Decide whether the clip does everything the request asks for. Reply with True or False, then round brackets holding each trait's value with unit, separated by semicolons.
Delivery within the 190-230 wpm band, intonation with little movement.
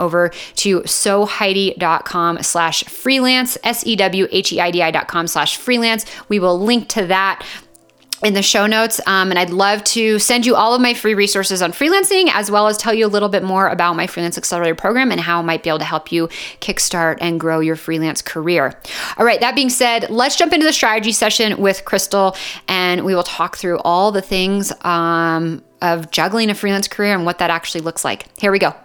False (200 wpm; 4.1 semitones)